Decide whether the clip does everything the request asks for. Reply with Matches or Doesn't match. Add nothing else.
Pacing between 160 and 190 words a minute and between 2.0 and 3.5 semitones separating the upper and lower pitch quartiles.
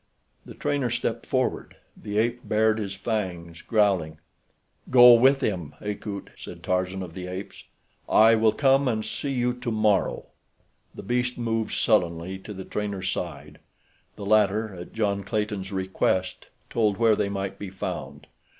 Doesn't match